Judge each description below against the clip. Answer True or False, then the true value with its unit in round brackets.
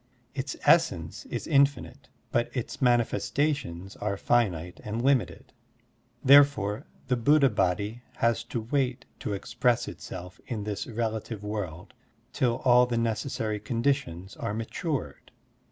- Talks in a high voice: False (115 Hz)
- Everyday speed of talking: False (120 wpm)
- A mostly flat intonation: False (4.1 semitones)